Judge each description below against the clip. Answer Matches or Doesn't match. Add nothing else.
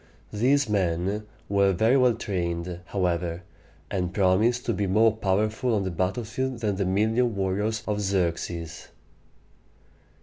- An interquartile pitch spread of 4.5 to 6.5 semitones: Doesn't match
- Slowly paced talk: Matches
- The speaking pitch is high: Doesn't match